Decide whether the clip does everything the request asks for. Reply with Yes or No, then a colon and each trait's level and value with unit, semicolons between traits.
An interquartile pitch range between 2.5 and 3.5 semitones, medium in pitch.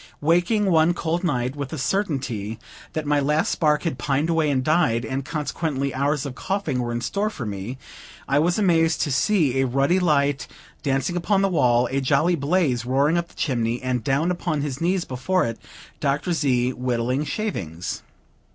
No: average, 4.8 semitones; medium, 145 Hz